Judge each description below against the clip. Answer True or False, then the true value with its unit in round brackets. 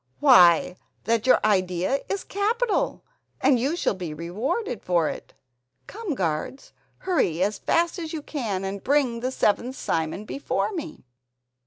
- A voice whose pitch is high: True (240 Hz)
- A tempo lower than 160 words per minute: True (145 wpm)